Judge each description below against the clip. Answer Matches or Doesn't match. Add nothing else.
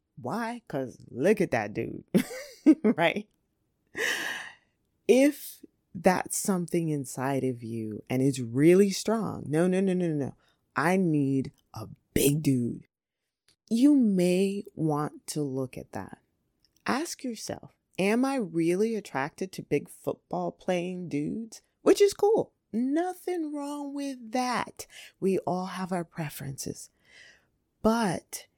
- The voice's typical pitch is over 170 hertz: Matches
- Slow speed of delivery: Matches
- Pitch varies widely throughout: Matches